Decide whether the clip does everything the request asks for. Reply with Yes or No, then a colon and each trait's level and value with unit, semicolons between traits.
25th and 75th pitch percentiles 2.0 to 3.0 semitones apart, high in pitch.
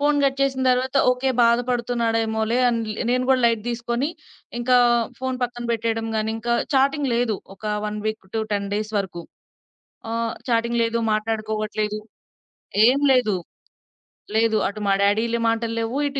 Yes: narrow, 2.4 semitones; high, 230 Hz